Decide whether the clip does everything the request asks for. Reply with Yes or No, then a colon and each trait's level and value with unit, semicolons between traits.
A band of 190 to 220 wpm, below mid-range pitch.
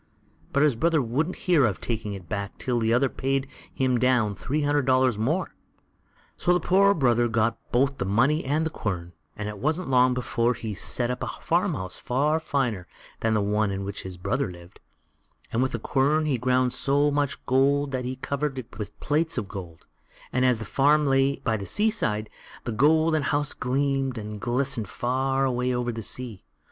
Yes: average, 195 wpm; low, 130 Hz